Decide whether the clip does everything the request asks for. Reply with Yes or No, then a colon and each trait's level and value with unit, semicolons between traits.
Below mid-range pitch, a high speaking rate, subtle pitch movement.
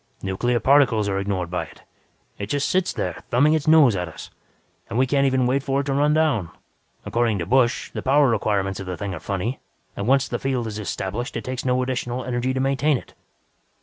No: low, 125 Hz; fast, 215 wpm; average, 5.1 semitones